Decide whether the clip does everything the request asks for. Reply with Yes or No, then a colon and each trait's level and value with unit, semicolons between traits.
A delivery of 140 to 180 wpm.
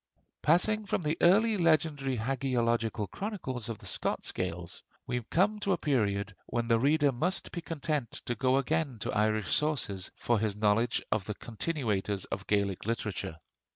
Yes: average, 160 wpm